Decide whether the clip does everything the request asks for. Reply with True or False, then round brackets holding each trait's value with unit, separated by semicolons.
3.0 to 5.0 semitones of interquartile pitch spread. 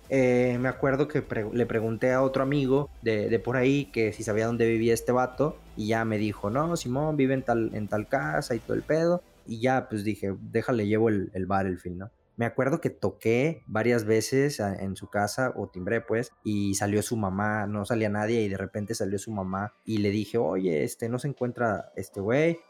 True (3.6 semitones)